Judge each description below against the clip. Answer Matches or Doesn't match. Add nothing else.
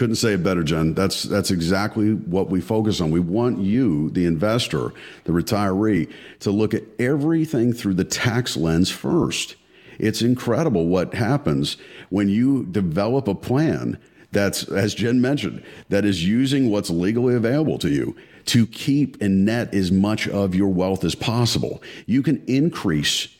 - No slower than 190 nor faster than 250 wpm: Doesn't match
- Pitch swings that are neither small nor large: Matches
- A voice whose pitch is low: Matches